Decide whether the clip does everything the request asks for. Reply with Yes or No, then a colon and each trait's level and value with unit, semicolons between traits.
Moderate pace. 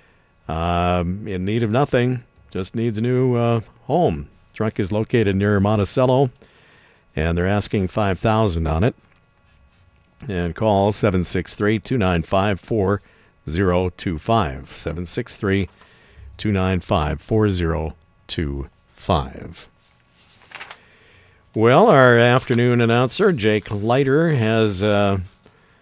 No: slow, 90 wpm